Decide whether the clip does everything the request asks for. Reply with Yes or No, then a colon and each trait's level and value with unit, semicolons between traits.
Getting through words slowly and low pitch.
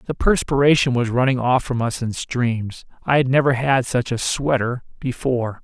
No: average, 170 wpm; low, 125 Hz